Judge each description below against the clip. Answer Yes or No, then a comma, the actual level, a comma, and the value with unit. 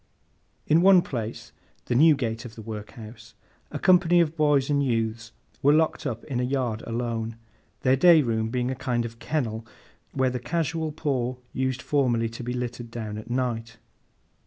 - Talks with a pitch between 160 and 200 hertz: No, low, 125 Hz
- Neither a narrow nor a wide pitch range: Yes, average, 3.9 semitones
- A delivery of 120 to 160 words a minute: No, average, 170 wpm